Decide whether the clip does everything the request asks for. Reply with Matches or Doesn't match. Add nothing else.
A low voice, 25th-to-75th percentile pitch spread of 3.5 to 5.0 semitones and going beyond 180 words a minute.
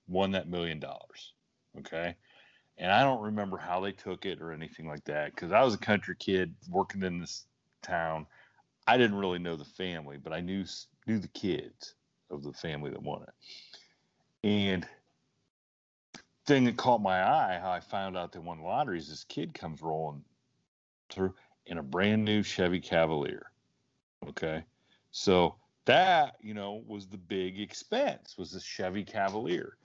Doesn't match